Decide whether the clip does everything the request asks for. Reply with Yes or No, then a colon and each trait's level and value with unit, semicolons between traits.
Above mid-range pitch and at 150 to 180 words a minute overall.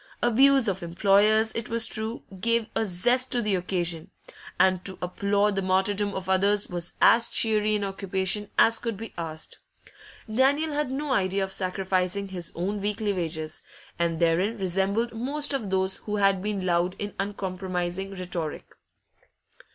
Yes: high, 195 Hz; average, 155 wpm